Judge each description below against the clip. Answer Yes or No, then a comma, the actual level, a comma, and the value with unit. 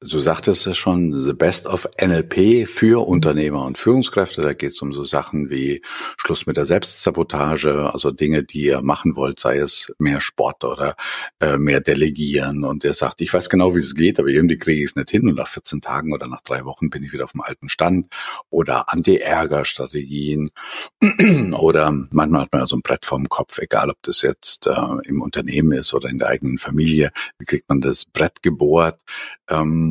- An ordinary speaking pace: No, fast, 200 wpm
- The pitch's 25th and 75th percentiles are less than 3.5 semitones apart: Yes, average, 2.7 semitones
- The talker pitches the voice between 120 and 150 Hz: No, very low, 75 Hz